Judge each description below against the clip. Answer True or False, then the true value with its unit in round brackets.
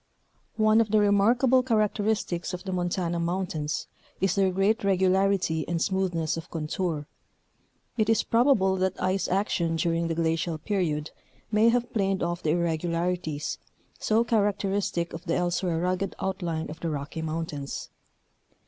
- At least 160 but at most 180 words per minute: False (145 wpm)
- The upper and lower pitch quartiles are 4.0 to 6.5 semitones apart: False (3.4 semitones)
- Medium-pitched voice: True (180 Hz)